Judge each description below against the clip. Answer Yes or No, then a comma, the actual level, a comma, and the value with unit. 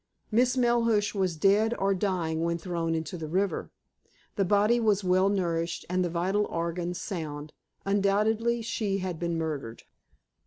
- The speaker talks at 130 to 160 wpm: Yes, average, 150 wpm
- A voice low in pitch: No, medium, 185 Hz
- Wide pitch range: No, average, 3.7 semitones